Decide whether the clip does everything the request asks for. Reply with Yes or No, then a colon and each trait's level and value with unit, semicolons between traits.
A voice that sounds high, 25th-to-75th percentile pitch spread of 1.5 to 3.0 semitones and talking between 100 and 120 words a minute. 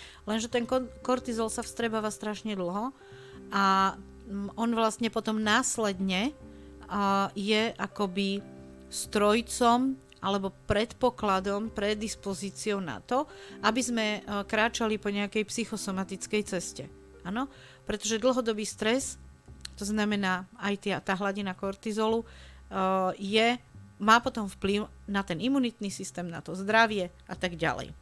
Yes: high, 205 Hz; narrow, 2.6 semitones; slow, 110 wpm